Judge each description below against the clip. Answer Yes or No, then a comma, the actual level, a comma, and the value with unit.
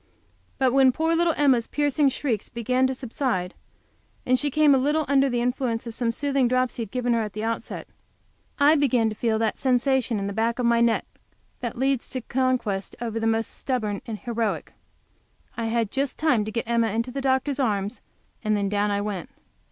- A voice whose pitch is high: Yes, high, 240 Hz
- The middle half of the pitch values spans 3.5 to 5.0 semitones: No, average, 3.0 semitones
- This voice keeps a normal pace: No, fast, 210 wpm